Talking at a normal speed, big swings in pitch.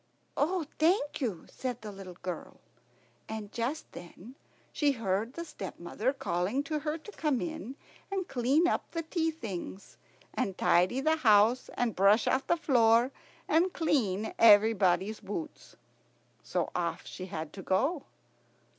Yes: average, 145 wpm; wide, 7.7 semitones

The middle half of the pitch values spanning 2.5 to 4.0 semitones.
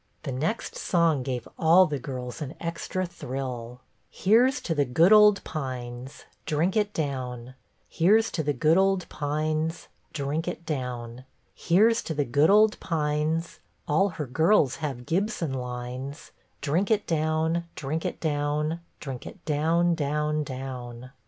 No: average, 4.4 semitones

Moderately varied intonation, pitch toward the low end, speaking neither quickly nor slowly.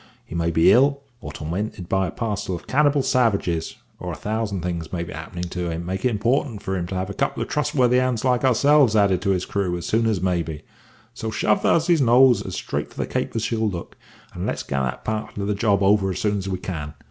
No: average, 5.0 semitones; low, 100 Hz; fast, 255 wpm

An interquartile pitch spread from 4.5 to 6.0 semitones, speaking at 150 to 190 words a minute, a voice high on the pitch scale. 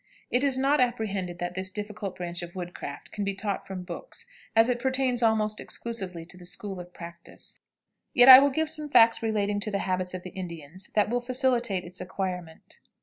No: average, 5.1 semitones; average, 200 wpm; high, 205 Hz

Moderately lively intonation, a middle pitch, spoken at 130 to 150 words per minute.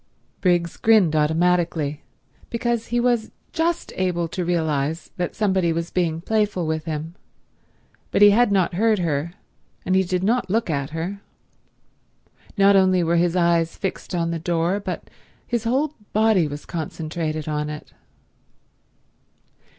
Yes: average, 3.9 semitones; medium, 175 Hz; average, 145 wpm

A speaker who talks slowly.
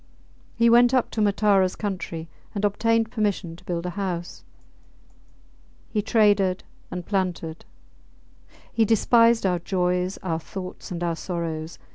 Yes: slow, 130 wpm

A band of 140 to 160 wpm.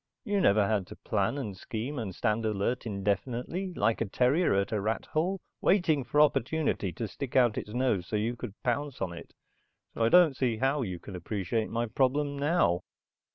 No: average, 195 wpm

